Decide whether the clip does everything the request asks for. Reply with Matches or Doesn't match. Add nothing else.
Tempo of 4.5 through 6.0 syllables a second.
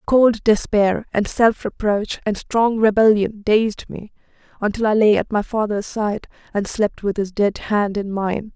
Doesn't match